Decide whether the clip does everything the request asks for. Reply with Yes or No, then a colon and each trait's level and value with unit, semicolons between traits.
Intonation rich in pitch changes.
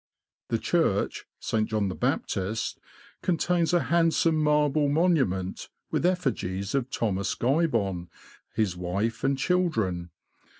Yes: wide, 8.8 semitones